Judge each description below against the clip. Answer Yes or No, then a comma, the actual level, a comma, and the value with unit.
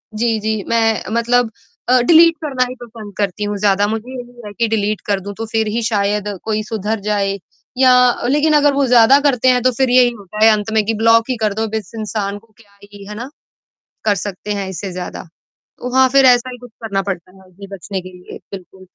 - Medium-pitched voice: No, high, 220 Hz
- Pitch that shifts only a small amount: No, average, 3.3 semitones